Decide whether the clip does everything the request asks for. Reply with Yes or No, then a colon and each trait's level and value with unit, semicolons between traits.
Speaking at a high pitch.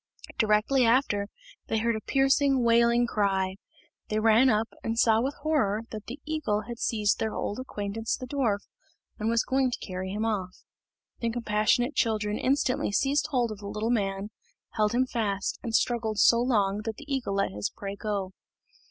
Yes: high, 225 Hz